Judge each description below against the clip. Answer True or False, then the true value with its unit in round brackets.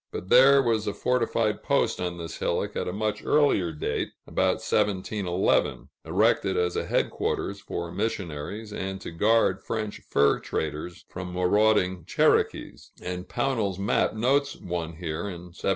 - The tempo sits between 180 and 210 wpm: False (150 wpm)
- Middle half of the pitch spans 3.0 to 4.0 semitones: True (3.7 semitones)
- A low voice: True (95 Hz)